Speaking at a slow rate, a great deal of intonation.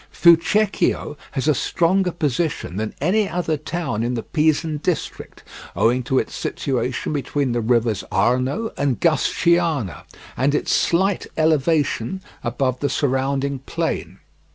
No: slow, 130 wpm; average, 4.9 semitones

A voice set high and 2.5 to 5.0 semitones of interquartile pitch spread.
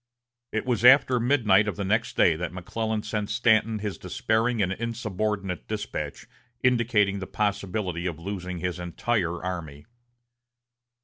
No: low, 105 Hz; average, 3.6 semitones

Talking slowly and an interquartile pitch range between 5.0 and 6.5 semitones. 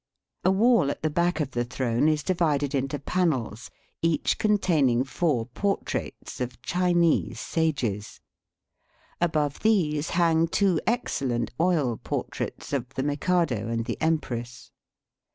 Yes: slow, 130 wpm; wide, 5.5 semitones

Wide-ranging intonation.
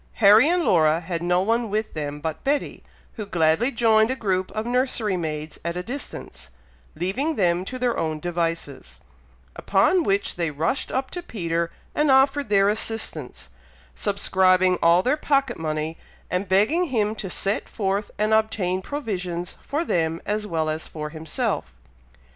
Yes: wide, 5.7 semitones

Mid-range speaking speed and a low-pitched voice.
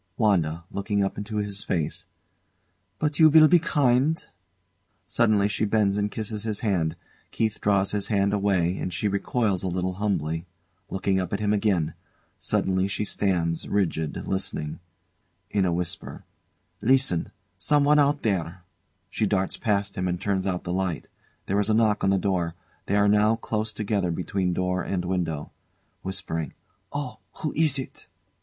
Yes: average, 160 wpm; low, 100 Hz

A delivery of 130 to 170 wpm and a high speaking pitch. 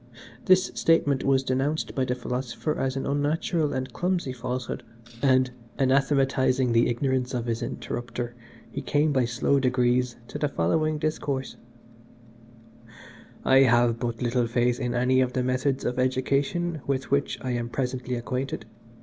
No: average, 150 wpm; low, 130 Hz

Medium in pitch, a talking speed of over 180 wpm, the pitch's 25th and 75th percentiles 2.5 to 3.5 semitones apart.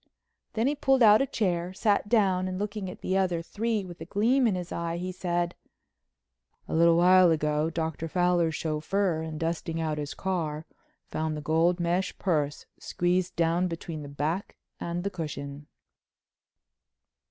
No: medium, 175 Hz; average, 160 wpm; average, 2.8 semitones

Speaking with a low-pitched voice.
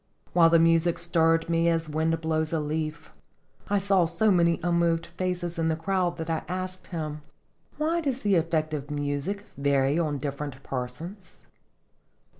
No: medium, 165 Hz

